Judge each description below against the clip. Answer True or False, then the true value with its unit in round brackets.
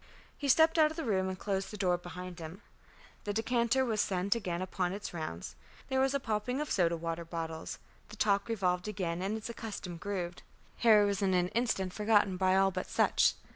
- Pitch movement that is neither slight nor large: True (3.7 semitones)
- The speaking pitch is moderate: False (195 Hz)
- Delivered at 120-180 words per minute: False (205 wpm)